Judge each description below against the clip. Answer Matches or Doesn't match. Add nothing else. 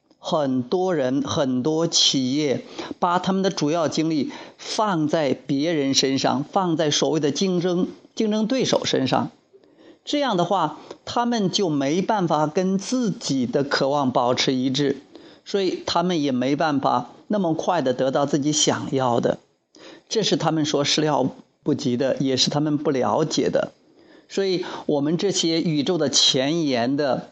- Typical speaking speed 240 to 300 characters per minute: Doesn't match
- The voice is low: Doesn't match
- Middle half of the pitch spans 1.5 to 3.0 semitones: Doesn't match